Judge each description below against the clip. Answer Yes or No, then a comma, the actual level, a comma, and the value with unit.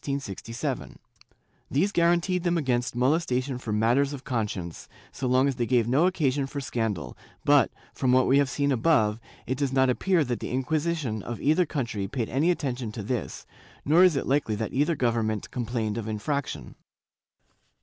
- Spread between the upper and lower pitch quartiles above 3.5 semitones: Yes, average, 3.9 semitones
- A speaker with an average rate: Yes, average, 175 wpm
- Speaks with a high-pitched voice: No, low, 130 Hz